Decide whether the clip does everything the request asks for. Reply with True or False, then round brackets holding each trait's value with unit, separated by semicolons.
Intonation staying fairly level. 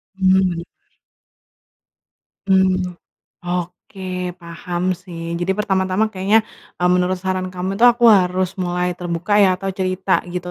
True (1.1 semitones)